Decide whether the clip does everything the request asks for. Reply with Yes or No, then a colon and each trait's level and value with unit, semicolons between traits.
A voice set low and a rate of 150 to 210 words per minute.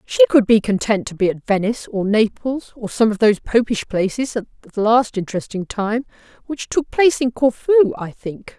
No: high, 230 Hz; average, 195 wpm